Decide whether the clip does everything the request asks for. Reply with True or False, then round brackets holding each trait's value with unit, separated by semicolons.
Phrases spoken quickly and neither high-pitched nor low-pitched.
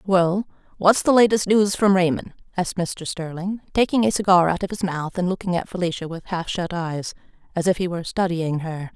True (210 wpm; 180 Hz)